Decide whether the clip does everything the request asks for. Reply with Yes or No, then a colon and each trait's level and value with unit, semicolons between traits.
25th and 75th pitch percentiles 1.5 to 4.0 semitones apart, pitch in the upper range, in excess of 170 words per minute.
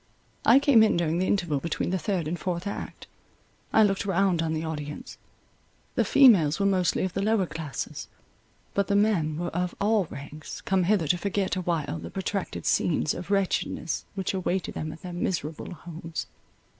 No: average, 3.5 semitones; medium, 180 Hz; average, 180 wpm